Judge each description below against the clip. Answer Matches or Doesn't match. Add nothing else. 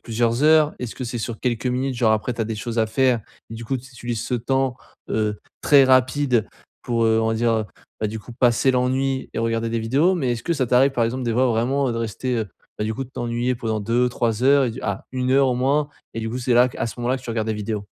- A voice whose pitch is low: Matches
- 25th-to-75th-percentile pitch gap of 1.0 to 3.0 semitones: Matches